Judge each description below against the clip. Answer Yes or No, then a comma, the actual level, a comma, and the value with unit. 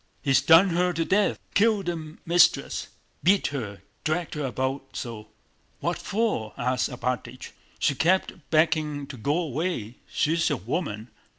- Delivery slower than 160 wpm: Yes, average, 140 wpm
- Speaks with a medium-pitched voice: Yes, medium, 150 Hz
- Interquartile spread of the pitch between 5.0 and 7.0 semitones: Yes, wide, 5.4 semitones